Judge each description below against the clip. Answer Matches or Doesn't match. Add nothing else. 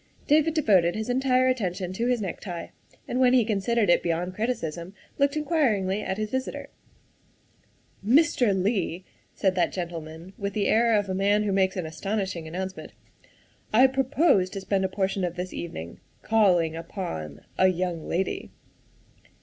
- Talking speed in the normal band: Matches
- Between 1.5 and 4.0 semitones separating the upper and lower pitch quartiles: Doesn't match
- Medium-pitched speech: Doesn't match